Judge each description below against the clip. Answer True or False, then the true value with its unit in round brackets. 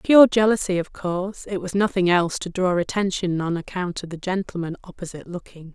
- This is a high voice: False (180 Hz)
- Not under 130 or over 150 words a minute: False (190 wpm)